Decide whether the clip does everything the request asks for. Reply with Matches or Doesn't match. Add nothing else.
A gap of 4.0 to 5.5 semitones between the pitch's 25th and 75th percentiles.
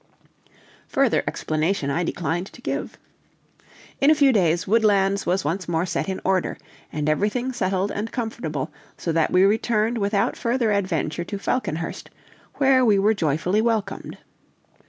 Matches